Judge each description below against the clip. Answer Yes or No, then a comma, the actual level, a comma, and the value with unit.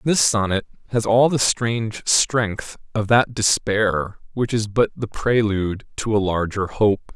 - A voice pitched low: Yes, low, 110 Hz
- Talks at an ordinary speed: Yes, average, 170 wpm